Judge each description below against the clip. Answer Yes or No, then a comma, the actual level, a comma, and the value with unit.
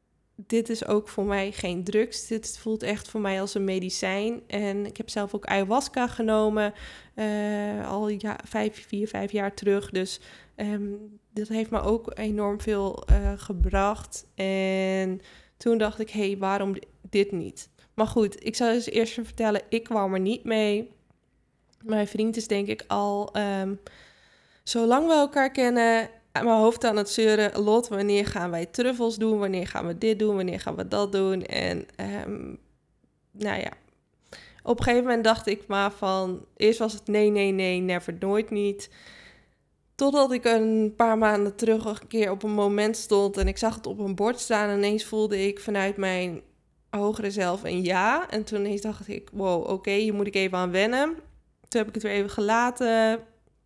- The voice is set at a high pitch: Yes, high, 210 Hz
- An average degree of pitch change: No, narrow, 2.0 semitones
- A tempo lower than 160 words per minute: No, average, 185 wpm